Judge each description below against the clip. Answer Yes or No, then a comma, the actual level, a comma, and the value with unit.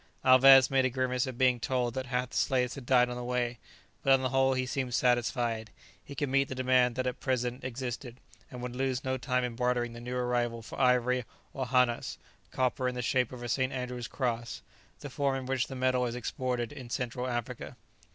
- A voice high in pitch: No, low, 125 Hz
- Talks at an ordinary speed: No, fast, 220 wpm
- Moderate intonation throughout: No, narrow, 1.1 semitones